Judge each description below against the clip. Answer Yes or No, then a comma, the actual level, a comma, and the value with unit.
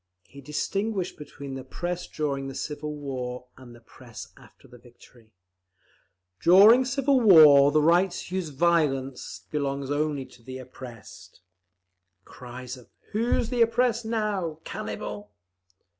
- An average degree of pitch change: No, wide, 6.3 semitones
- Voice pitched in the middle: Yes, medium, 145 Hz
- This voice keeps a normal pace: No, slow, 130 wpm